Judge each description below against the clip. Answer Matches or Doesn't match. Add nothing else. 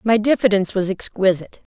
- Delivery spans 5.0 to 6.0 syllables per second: Doesn't match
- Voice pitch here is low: Doesn't match